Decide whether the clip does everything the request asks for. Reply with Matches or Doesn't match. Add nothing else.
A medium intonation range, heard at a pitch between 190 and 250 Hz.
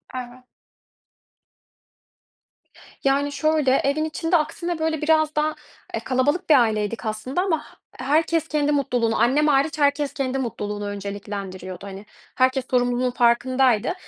Doesn't match